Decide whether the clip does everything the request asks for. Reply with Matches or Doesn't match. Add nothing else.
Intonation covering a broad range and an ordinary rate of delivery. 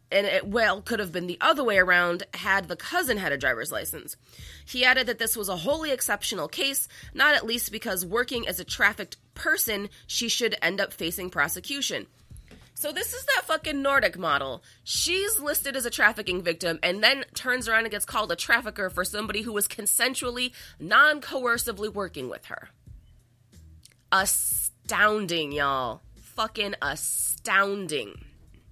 Matches